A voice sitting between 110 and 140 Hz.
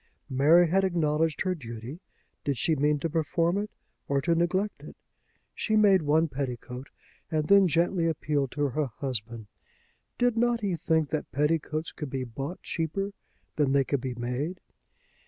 No: medium, 155 Hz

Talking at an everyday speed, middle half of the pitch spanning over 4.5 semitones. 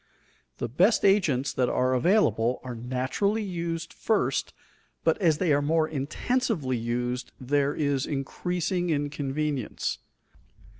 No: slow, 115 wpm; wide, 5.4 semitones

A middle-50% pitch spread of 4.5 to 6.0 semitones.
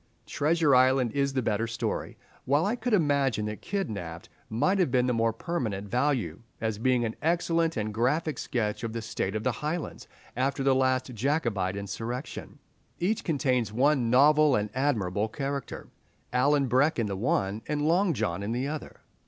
Yes: average, 4.9 semitones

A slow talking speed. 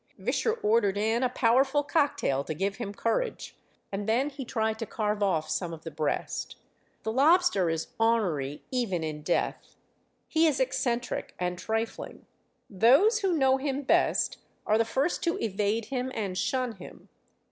No: average, 160 wpm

